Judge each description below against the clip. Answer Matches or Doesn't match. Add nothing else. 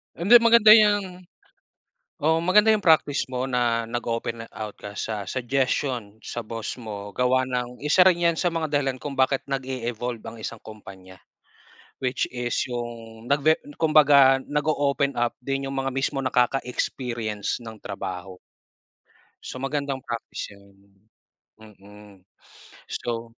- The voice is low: Matches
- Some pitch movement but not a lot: Matches